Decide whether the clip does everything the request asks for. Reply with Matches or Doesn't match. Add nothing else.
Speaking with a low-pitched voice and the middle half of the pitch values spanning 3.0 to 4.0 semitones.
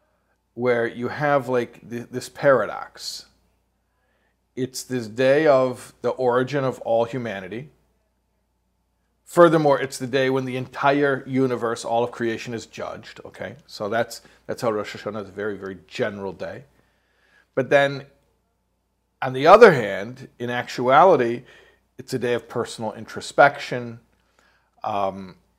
Matches